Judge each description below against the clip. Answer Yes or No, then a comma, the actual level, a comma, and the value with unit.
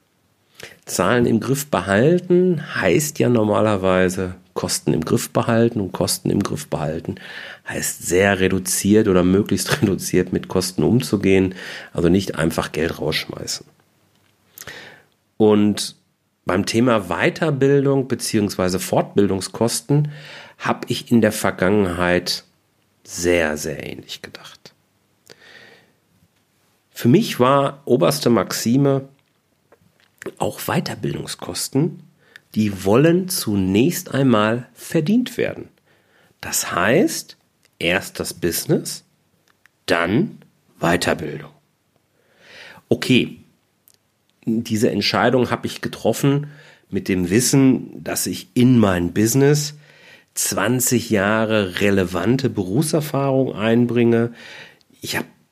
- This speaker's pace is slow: Yes, slow, 95 wpm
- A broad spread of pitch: Yes, wide, 5.9 semitones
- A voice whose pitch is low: Yes, low, 115 Hz